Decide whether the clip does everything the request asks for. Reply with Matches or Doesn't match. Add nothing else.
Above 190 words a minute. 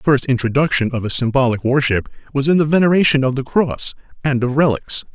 Matches